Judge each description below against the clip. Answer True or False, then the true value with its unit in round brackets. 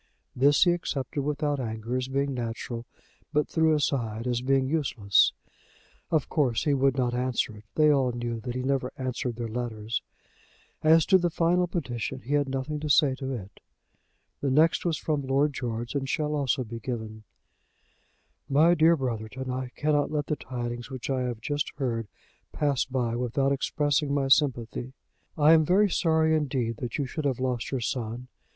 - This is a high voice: False (135 Hz)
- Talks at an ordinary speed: True (175 wpm)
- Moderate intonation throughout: True (3.5 semitones)